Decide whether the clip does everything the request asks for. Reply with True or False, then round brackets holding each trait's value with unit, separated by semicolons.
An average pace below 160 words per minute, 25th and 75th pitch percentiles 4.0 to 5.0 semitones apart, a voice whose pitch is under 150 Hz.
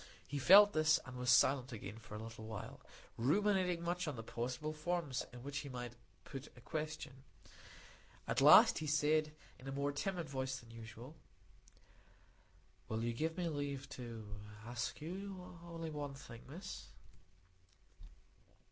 True (150 wpm; 4.6 semitones; 140 Hz)